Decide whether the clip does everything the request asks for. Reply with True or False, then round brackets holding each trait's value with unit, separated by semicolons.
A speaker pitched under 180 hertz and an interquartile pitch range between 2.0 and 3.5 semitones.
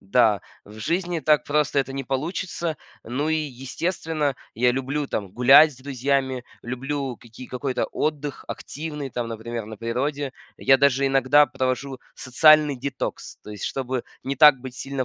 True (135 Hz; 2.9 semitones)